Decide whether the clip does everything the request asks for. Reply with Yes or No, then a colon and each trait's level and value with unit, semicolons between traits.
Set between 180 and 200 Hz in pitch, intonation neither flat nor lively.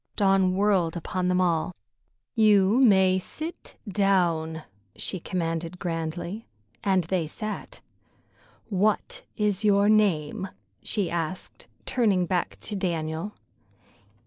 Yes: medium, 185 Hz; average, 3.3 semitones